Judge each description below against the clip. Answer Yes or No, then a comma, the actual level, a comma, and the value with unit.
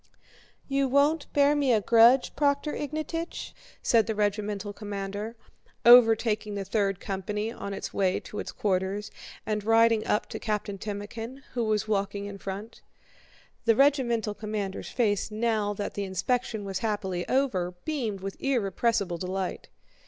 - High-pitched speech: Yes, high, 215 Hz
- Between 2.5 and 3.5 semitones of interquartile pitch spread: Yes, average, 3.1 semitones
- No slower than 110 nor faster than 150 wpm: Yes, average, 145 wpm